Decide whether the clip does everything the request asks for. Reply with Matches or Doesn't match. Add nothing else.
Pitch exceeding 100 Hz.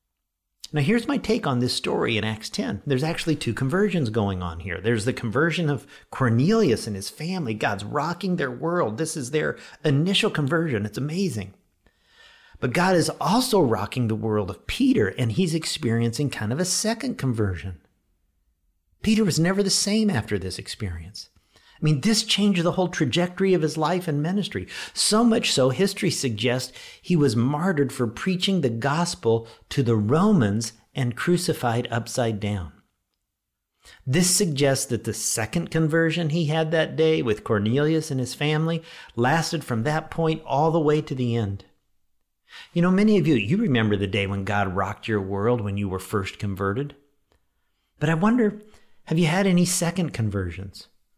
Matches